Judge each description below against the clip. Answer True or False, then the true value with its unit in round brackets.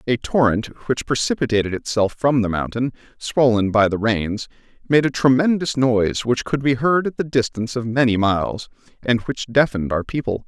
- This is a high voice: False (120 Hz)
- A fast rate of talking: False (180 wpm)